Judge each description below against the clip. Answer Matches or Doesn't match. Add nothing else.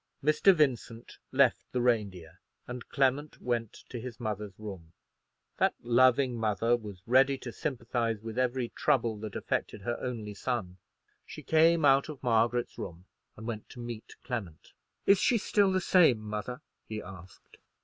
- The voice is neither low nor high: Doesn't match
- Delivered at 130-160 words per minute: Matches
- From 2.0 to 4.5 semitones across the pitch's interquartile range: Matches